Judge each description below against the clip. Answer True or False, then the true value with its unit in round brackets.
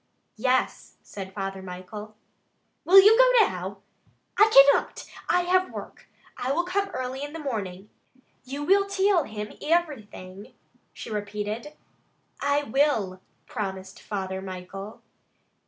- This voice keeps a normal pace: False (120 wpm)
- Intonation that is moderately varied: False (9.0 semitones)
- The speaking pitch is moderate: False (225 Hz)